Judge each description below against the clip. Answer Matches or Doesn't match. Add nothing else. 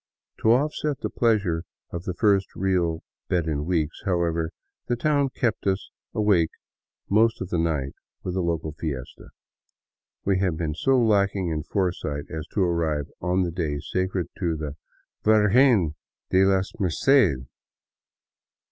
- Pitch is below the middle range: Matches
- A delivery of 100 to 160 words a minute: Matches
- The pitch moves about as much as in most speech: Matches